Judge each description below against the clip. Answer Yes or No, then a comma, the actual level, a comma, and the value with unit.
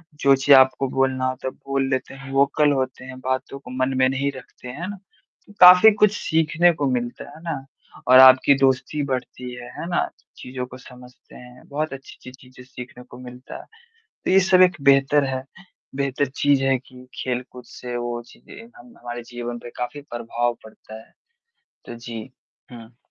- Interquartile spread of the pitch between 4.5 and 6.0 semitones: No, narrow, 2.4 semitones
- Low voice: Yes, low, 130 Hz